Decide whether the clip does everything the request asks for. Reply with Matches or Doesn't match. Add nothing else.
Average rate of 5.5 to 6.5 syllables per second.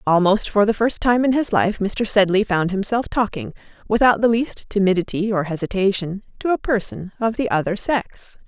Doesn't match